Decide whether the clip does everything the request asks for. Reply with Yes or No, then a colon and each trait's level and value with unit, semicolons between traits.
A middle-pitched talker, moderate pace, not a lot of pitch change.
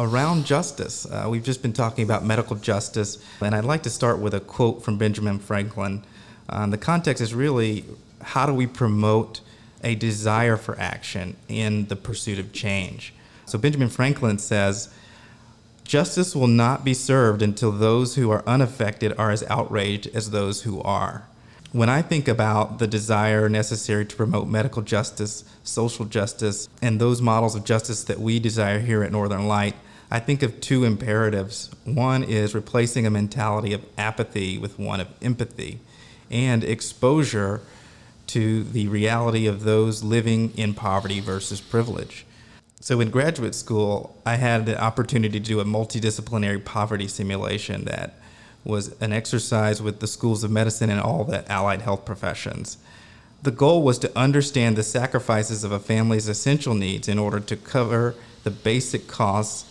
No: low, 110 Hz; average, 160 wpm; narrow, 2.1 semitones